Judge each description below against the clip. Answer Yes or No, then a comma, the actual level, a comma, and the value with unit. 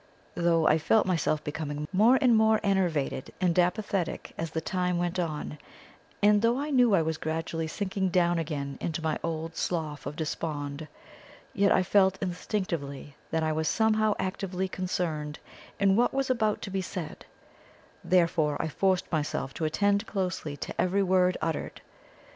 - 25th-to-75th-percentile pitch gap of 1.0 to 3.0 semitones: No, average, 3.8 semitones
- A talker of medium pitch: Yes, medium, 175 Hz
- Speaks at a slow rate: No, average, 160 wpm